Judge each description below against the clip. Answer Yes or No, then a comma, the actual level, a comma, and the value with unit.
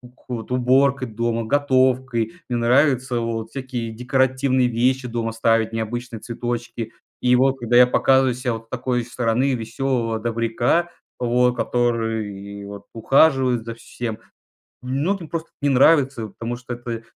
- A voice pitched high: No, low, 120 Hz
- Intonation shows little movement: Yes, narrow, 2.3 semitones